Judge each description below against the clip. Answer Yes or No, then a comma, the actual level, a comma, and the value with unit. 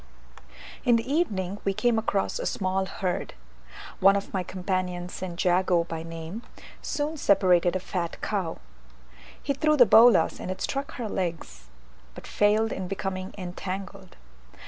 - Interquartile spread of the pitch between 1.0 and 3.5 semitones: Yes, average, 3.1 semitones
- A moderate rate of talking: Yes, average, 145 wpm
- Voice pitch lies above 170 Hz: Yes, high, 190 Hz